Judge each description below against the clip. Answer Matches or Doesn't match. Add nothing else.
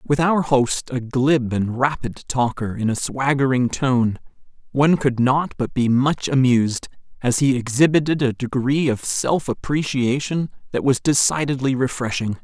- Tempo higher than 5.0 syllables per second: Doesn't match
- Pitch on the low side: Matches